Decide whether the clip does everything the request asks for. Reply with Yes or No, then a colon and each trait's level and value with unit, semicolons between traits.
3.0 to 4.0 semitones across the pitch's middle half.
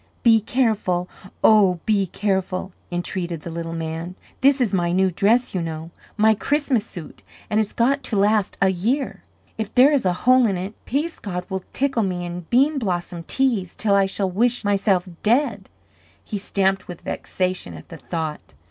No: average, 4.6 semitones